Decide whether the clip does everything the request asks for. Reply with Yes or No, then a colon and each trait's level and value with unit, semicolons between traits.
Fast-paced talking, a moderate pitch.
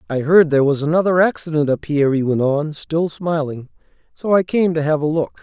Yes: fast, 220 wpm; medium, 155 Hz